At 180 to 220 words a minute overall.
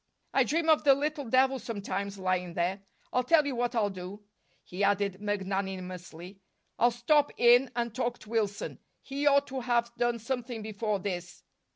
No: average, 170 wpm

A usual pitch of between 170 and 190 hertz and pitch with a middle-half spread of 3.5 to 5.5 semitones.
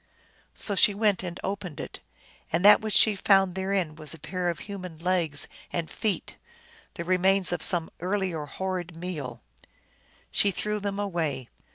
No: medium, 185 Hz; average, 2.9 semitones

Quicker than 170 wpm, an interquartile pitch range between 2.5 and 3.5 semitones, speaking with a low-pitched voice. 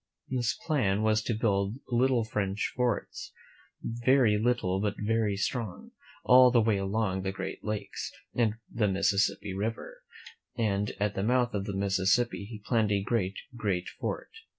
No: average, 150 wpm; average, 3.1 semitones; low, 105 Hz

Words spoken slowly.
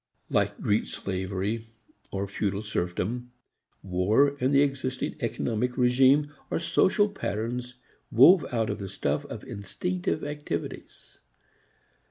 Yes: slow, 115 wpm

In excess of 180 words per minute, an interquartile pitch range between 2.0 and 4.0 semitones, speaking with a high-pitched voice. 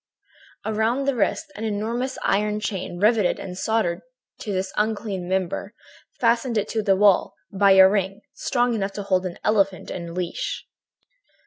No: average, 155 wpm; average, 2.7 semitones; high, 205 Hz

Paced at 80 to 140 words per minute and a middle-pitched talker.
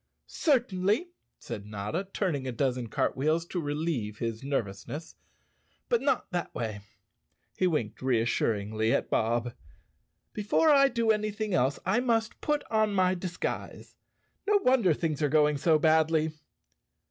Yes: slow, 135 wpm; medium, 160 Hz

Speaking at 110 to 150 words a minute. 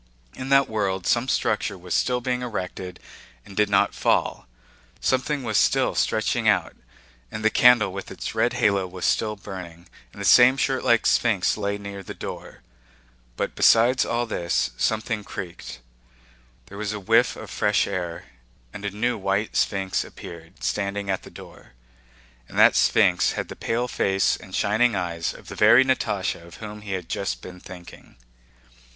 No: average, 170 wpm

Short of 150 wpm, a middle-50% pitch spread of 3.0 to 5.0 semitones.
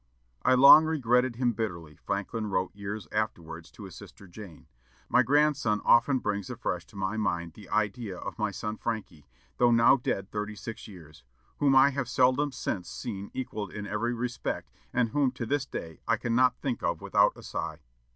No: average, 180 wpm; average, 4.2 semitones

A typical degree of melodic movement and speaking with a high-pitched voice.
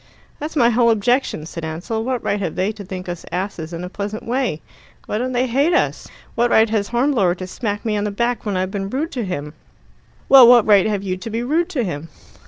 Yes: average, 4.7 semitones; high, 215 Hz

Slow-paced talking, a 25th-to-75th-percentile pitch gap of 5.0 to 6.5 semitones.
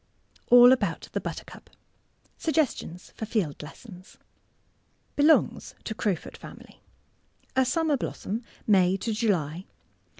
Yes: slow, 105 wpm; wide, 5.6 semitones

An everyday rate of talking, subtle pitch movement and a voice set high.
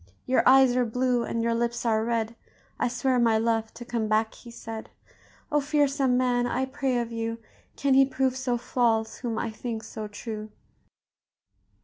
Yes: average, 175 wpm; narrow, 2.3 semitones; high, 235 Hz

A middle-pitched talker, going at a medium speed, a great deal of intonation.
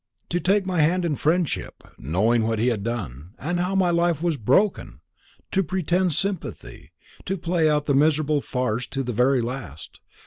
Yes: medium, 150 Hz; average, 175 wpm; wide, 6.5 semitones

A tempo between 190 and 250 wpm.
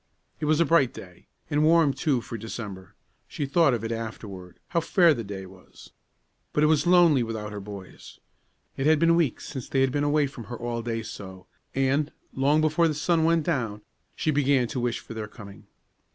Yes: fast, 205 wpm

